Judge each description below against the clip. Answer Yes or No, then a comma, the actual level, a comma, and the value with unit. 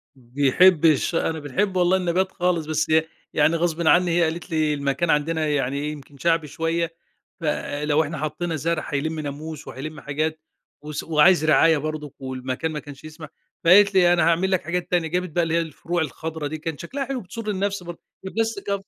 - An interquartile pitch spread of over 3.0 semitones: No, narrow, 2.6 semitones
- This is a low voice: No, medium, 160 Hz